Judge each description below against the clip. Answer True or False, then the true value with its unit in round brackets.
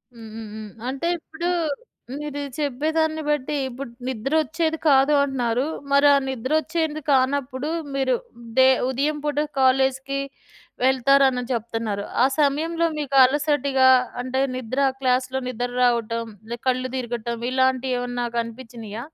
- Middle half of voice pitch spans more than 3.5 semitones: False (2.8 semitones)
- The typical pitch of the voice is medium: False (260 Hz)